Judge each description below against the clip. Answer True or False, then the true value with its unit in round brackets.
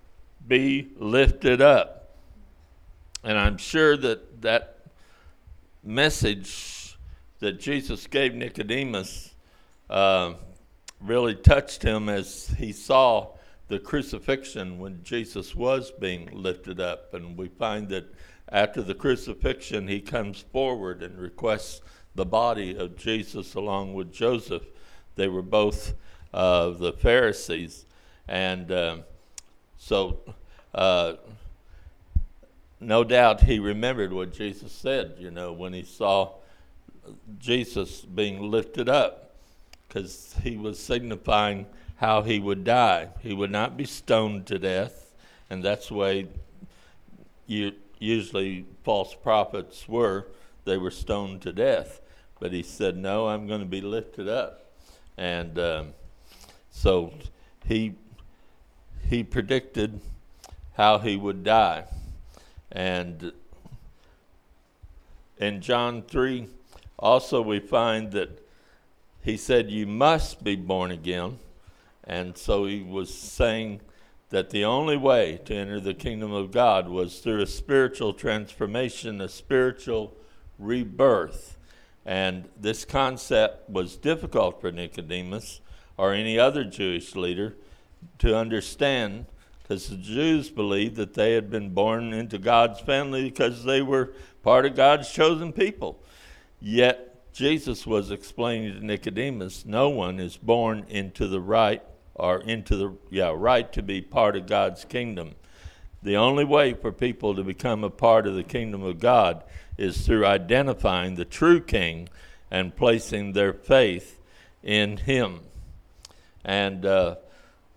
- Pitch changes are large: False (4.0 semitones)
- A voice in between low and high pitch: False (100 Hz)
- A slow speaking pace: True (125 wpm)